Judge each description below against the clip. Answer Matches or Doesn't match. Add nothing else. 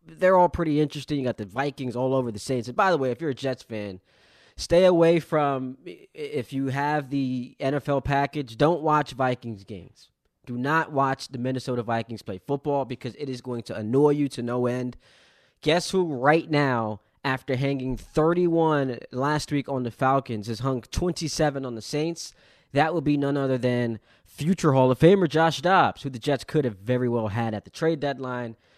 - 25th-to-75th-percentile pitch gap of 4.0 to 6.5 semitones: Doesn't match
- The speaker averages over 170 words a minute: Matches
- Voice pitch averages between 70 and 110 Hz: Doesn't match